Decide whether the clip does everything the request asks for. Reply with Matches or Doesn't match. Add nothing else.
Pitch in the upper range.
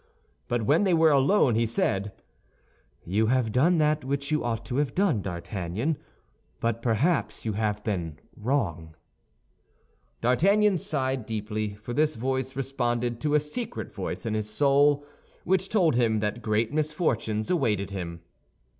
Doesn't match